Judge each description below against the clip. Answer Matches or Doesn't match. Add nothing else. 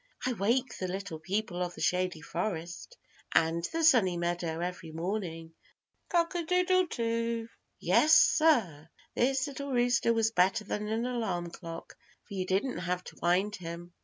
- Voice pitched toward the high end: Matches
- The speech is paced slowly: Doesn't match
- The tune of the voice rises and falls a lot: Matches